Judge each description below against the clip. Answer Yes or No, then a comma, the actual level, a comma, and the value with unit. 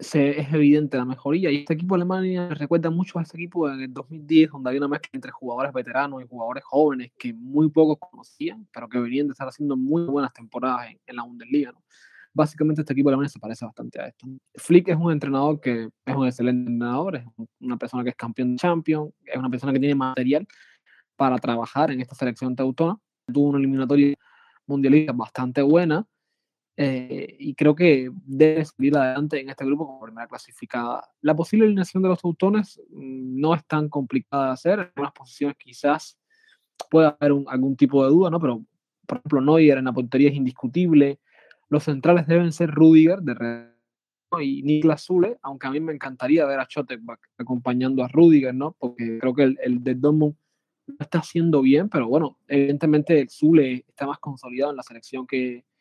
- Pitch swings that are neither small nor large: Yes, average, 3.5 semitones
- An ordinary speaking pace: No, fast, 195 wpm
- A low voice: No, medium, 145 Hz